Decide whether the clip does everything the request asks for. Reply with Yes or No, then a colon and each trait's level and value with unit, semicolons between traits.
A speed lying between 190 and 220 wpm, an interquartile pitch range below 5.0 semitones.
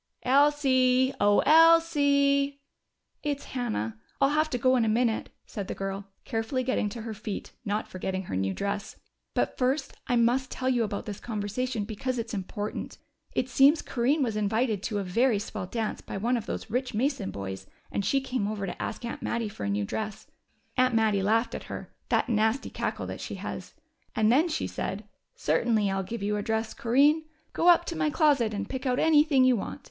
Yes: average, 200 wpm; average, 4.5 semitones